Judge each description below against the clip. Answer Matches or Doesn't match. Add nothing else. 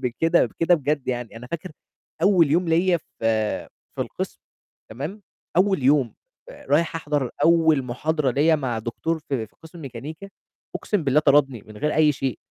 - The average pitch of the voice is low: Doesn't match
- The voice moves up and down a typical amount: Matches